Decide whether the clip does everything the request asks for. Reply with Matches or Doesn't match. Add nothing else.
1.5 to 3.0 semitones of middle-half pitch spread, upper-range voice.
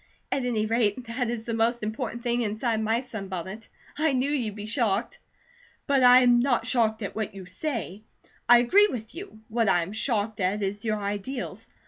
Matches